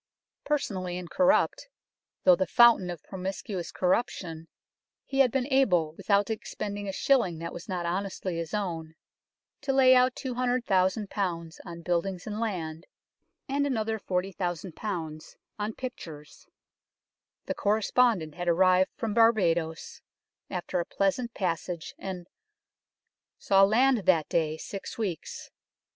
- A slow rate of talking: Yes, slow, 125 wpm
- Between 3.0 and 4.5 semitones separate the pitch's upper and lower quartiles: No, average, 4.9 semitones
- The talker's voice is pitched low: No, high, 190 Hz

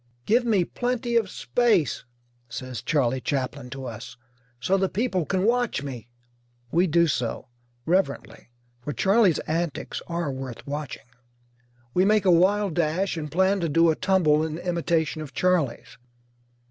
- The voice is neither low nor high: Yes, medium, 170 Hz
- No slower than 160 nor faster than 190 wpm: No, average, 145 wpm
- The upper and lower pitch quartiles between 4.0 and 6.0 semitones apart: Yes, average, 5.2 semitones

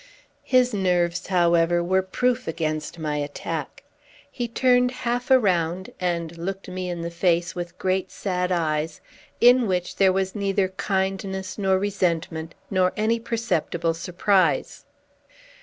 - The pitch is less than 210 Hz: Yes, medium, 185 Hz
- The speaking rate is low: Yes, slow, 130 wpm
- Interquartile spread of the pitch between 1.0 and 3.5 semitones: Yes, average, 2.8 semitones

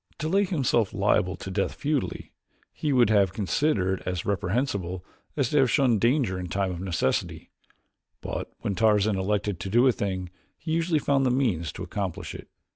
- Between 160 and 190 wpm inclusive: Yes, average, 180 wpm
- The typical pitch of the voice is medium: No, low, 105 Hz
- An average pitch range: No, wide, 6.0 semitones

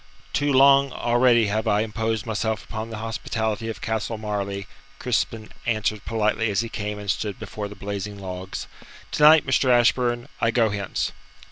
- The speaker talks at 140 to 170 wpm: Yes, average, 165 wpm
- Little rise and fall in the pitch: Yes, narrow, 2.3 semitones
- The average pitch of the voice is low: Yes, low, 110 Hz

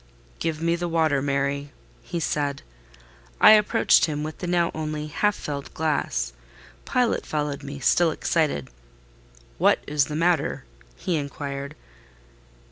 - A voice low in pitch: No, medium, 150 Hz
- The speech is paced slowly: Yes, slow, 130 wpm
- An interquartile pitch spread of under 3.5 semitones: Yes, average, 2.9 semitones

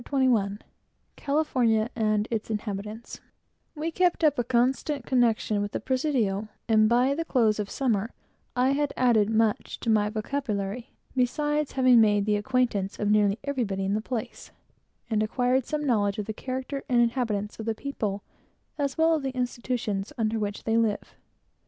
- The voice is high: Yes, high, 230 Hz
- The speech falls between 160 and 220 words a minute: Yes, average, 170 wpm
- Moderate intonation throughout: Yes, average, 3.8 semitones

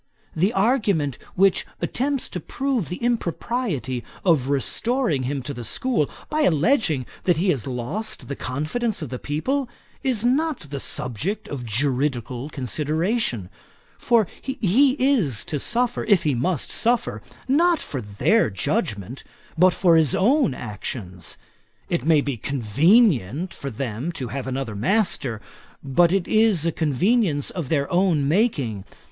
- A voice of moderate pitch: Yes, medium, 160 Hz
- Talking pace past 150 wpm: No, average, 140 wpm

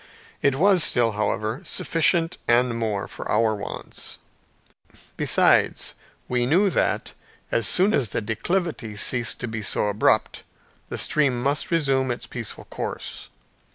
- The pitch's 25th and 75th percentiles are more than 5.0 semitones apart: Yes, wide, 5.6 semitones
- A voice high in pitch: No, low, 125 Hz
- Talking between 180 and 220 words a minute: No, slow, 135 wpm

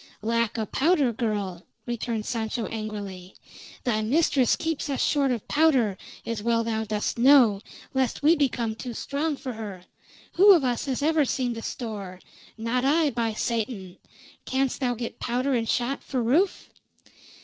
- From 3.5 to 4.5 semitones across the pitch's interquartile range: Yes, average, 3.8 semitones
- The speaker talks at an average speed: Yes, average, 160 wpm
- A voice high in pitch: Yes, high, 240 Hz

